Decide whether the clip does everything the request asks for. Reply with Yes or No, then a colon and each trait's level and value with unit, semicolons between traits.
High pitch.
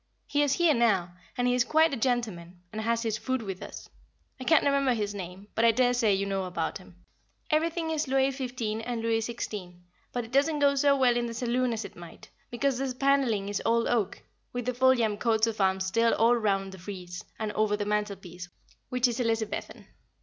Yes: high, 230 Hz